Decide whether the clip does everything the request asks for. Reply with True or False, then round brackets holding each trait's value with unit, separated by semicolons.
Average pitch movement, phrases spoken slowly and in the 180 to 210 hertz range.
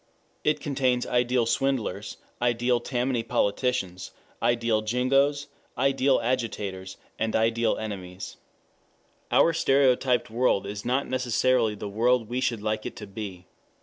False (3.1 semitones; 115 wpm; 120 Hz)